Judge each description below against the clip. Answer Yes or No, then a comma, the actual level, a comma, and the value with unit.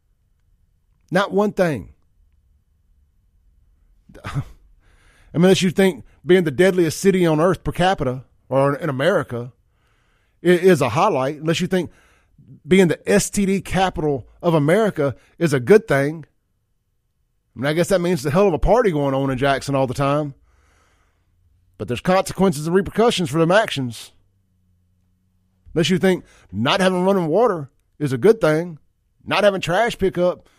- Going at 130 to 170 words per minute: Yes, average, 145 wpm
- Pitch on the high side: No, medium, 140 Hz